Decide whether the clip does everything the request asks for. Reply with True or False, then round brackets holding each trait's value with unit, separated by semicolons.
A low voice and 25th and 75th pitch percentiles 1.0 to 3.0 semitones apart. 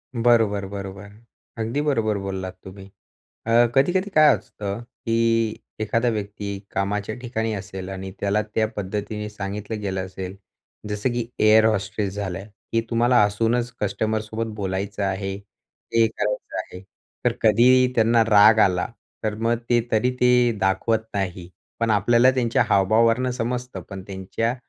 True (110 Hz; 2.7 semitones)